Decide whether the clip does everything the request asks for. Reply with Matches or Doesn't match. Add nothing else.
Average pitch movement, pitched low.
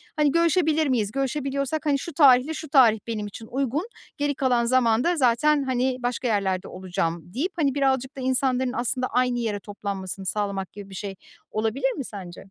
Doesn't match